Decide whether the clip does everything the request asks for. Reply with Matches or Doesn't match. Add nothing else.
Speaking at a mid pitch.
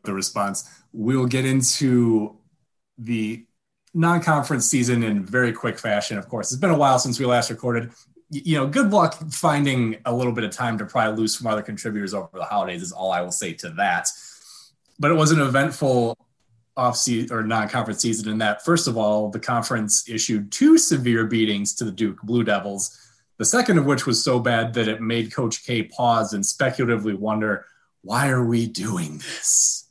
Doesn't match